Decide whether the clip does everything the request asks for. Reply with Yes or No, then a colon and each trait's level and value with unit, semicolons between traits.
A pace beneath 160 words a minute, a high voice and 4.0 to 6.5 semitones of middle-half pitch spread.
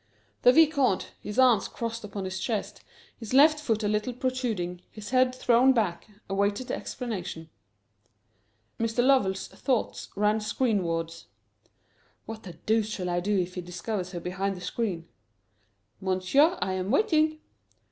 Yes: average, 145 wpm; high, 210 Hz; average, 5.1 semitones